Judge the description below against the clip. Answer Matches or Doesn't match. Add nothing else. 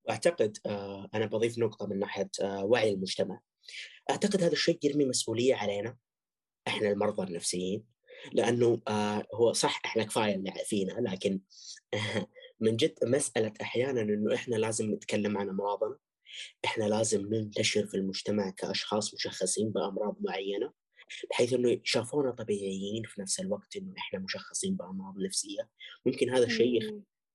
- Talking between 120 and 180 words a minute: Matches